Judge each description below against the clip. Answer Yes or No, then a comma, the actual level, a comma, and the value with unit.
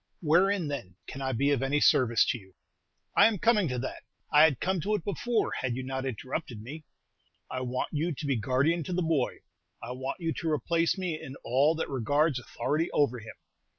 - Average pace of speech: No, fast, 210 wpm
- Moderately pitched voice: Yes, medium, 145 Hz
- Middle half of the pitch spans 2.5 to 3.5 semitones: No, average, 4.5 semitones